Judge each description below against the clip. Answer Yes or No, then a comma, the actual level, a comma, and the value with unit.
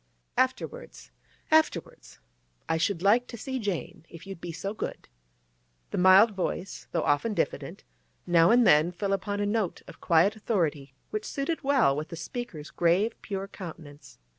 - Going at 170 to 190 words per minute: No, average, 155 wpm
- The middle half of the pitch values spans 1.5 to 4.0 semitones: No, average, 5.0 semitones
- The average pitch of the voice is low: No, high, 195 Hz